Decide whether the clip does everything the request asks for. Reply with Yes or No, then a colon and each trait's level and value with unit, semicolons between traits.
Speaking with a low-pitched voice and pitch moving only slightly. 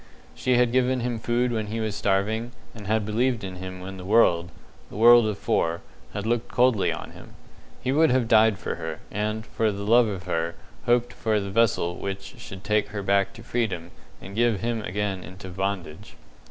No: low, 105 Hz; average, 3.4 semitones